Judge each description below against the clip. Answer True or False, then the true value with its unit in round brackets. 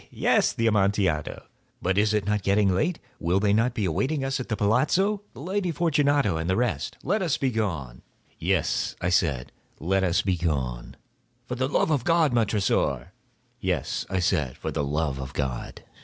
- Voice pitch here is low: True (100 Hz)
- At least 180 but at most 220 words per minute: True (185 wpm)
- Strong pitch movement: True (8.0 semitones)